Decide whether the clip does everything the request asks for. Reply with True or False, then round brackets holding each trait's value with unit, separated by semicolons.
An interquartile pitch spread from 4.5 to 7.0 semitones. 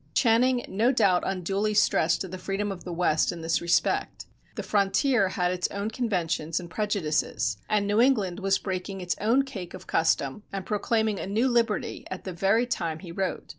False (3.5 semitones)